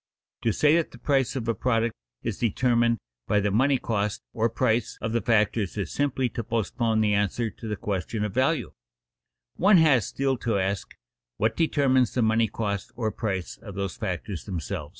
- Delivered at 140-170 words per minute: No, average, 185 wpm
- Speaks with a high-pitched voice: No, low, 115 Hz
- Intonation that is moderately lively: Yes, average, 3.5 semitones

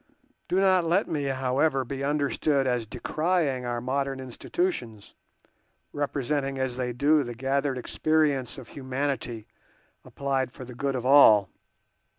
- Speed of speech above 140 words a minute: No, slow, 135 wpm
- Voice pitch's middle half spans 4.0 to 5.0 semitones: No, narrow, 2.5 semitones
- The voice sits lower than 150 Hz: Yes, low, 135 Hz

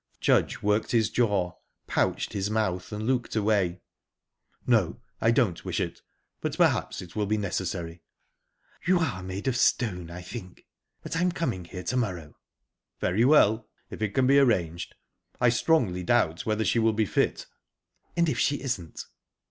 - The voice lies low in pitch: Yes, low, 105 Hz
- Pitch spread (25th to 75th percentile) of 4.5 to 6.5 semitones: Yes, average, 4.9 semitones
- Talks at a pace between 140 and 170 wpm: Yes, average, 165 wpm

